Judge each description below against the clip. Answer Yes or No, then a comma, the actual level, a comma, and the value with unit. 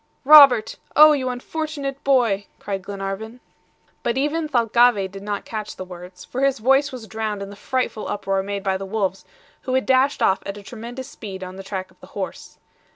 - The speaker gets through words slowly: No, average, 195 wpm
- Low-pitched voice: No, high, 220 Hz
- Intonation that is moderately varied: Yes, average, 5.0 semitones